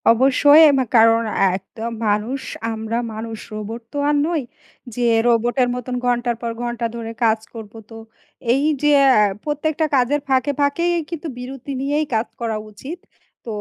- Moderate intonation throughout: Yes, average, 3.9 semitones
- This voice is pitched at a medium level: No, high, 245 Hz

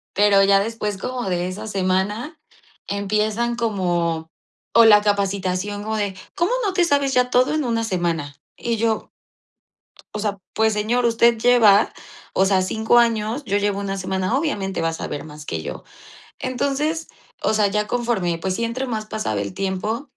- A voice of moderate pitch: No, high, 210 Hz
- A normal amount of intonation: Yes, average, 3.7 semitones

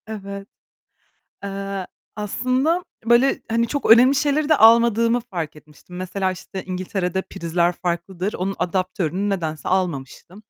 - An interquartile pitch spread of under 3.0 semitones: No, average, 4.4 semitones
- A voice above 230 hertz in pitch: No, high, 195 Hz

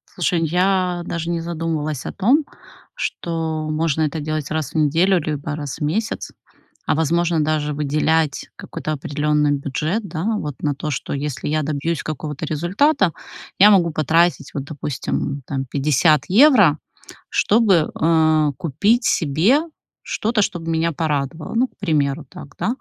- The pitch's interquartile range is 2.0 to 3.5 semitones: Yes, average, 2.7 semitones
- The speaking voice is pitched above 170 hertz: No, medium, 155 Hz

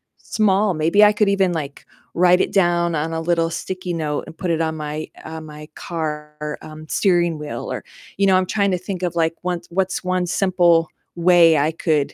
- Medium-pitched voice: Yes, medium, 170 Hz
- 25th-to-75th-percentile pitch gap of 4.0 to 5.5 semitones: No, average, 2.8 semitones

